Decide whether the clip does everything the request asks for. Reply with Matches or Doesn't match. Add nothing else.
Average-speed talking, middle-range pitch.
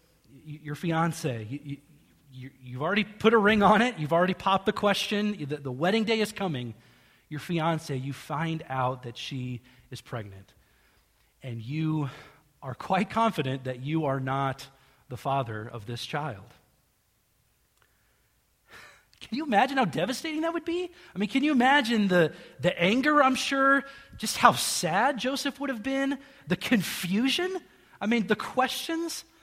Matches